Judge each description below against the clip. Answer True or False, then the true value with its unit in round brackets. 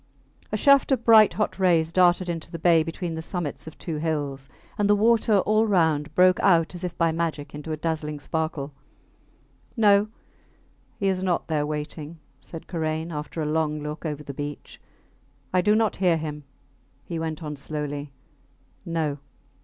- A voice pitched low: False (165 Hz)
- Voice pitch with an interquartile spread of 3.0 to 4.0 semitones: True (3.3 semitones)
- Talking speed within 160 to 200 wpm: True (170 wpm)